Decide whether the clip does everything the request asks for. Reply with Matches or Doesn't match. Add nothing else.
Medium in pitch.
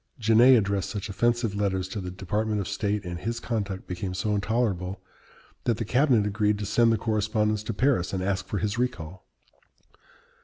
Doesn't match